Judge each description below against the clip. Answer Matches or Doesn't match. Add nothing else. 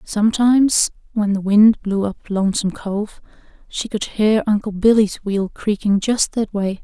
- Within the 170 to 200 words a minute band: Doesn't match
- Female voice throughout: Matches